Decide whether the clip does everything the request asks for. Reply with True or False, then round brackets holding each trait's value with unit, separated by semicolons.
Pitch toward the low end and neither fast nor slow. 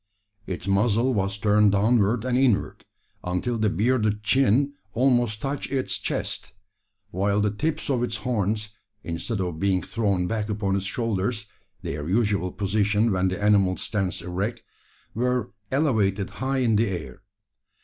True (105 Hz; 145 wpm)